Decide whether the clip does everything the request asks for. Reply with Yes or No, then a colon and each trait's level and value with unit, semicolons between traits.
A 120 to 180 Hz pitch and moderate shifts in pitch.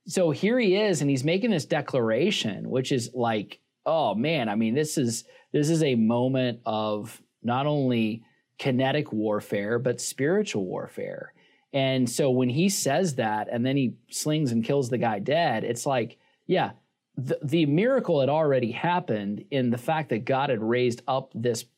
Yes: low, 135 Hz; average, 4.9 semitones